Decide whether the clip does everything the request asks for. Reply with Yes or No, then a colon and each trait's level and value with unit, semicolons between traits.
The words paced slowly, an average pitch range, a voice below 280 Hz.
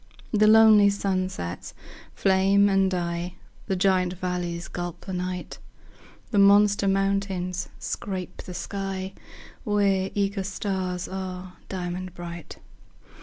No: slow, 110 wpm; narrow, 1.7 semitones; high, 190 Hz